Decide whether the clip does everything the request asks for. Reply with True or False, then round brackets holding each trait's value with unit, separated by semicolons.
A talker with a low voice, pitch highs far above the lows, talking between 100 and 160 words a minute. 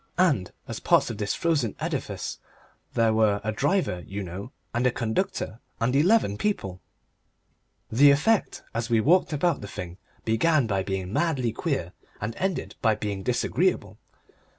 True (115 Hz; 6.9 semitones; 150 wpm)